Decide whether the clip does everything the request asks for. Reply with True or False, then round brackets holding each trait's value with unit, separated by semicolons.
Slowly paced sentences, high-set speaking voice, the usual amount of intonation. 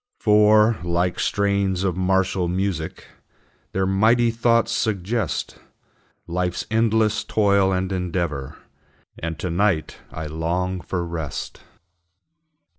False (105 wpm; 95 Hz; 3.4 semitones)